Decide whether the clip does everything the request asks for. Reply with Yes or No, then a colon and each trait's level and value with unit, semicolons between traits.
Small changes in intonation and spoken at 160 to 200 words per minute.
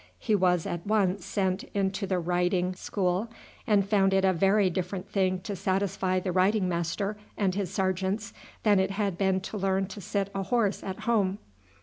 Yes: narrow, 1.5 semitones; average, 190 wpm